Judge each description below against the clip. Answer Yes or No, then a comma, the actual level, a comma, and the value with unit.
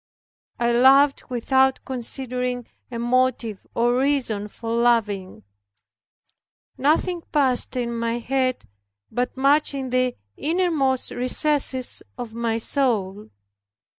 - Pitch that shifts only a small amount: Yes, narrow, 2.3 semitones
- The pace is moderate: No, slow, 105 wpm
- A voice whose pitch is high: Yes, very high, 250 Hz